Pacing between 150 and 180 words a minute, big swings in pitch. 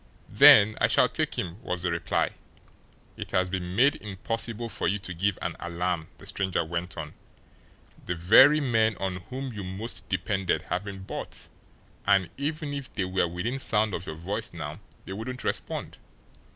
No: average, 175 wpm; average, 4.1 semitones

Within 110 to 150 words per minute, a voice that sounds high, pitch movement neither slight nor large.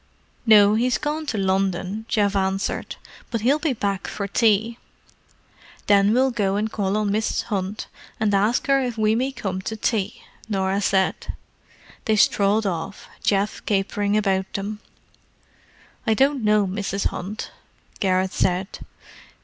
No: average, 140 wpm; high, 205 Hz; narrow, 2.3 semitones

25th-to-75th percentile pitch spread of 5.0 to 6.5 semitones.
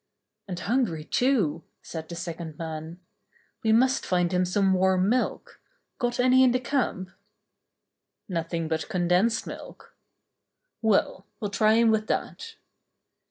Yes: wide, 5.4 semitones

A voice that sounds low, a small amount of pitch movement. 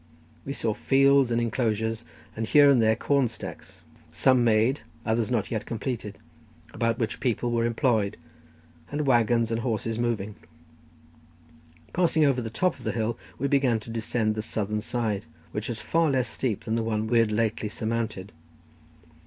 Yes: low, 115 Hz; narrow, 2.3 semitones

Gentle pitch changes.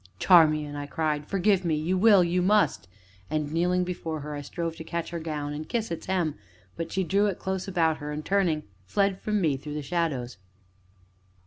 No: average, 3.7 semitones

